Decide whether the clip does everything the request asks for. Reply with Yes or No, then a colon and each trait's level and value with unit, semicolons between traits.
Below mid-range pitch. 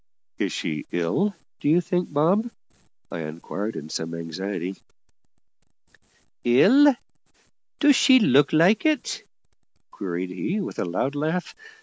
No: medium, 145 Hz